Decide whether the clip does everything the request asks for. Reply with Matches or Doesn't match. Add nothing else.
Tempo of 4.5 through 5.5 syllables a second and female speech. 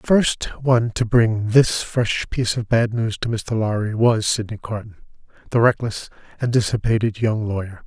Doesn't match